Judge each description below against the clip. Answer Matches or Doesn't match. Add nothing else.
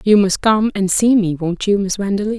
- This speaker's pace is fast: Matches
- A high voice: Matches